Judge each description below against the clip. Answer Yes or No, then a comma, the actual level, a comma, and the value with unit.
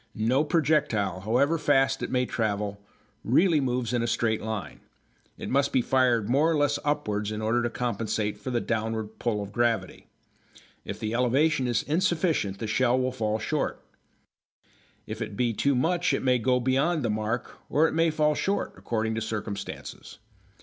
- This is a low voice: Yes, low, 120 Hz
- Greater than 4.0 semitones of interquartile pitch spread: Yes, average, 4.4 semitones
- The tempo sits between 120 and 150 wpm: No, average, 175 wpm